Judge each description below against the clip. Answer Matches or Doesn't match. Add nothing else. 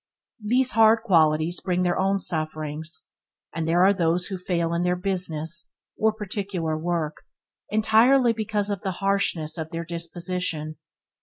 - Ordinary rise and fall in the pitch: Matches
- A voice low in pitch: Doesn't match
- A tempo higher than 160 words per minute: Doesn't match